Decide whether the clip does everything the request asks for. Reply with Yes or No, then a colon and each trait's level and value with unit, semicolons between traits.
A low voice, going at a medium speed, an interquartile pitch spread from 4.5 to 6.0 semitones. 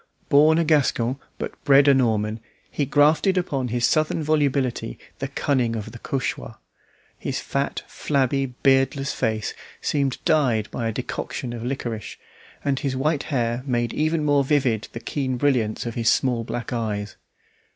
No: low, 130 Hz; average, 155 wpm; average, 3.6 semitones